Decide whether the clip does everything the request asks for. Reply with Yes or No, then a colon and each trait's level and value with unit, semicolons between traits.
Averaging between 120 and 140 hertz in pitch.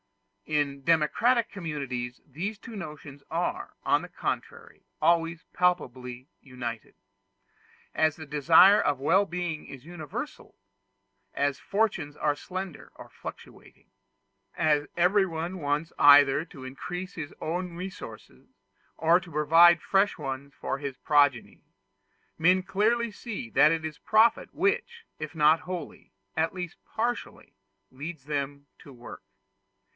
No: medium, 160 Hz